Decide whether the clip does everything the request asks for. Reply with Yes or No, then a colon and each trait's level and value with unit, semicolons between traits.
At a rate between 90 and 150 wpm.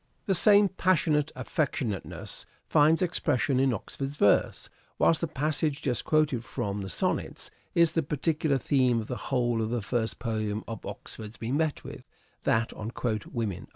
No: average, 160 wpm